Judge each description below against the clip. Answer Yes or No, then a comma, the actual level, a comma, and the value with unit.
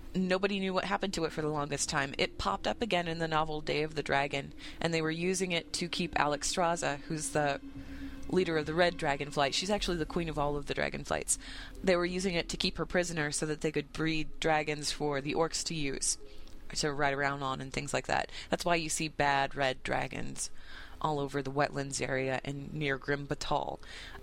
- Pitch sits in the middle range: Yes, medium, 150 Hz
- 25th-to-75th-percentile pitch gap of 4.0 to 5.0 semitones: No, average, 3.3 semitones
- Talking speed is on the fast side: Yes, fast, 225 wpm